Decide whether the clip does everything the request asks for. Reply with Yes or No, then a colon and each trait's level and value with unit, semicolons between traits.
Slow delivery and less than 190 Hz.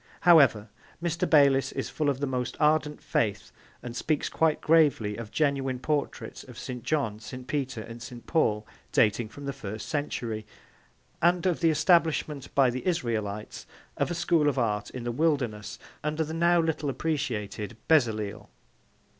No: average, 160 wpm; low, 135 Hz